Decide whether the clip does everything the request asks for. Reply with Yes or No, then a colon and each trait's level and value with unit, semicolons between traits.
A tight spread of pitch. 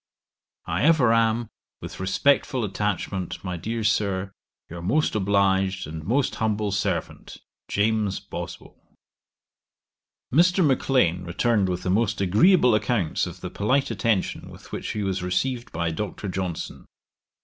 No: average, 3.9 semitones